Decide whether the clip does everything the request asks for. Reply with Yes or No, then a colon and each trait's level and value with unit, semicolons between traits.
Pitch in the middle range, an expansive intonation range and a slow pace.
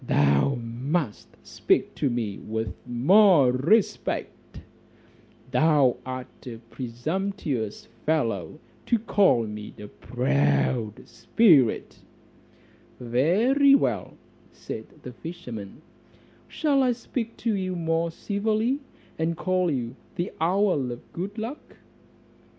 Yes: medium, 145 Hz; wide, 8.9 semitones; slow, 105 wpm